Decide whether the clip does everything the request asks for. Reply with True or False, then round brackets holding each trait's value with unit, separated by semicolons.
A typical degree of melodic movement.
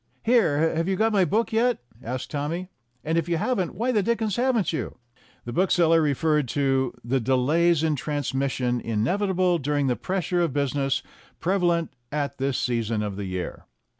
False (5.8 semitones)